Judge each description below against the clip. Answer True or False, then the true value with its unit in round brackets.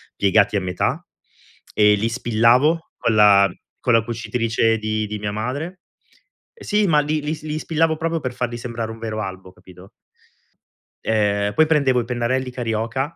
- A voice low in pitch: True (115 Hz)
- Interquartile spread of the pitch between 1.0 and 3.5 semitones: False (5.1 semitones)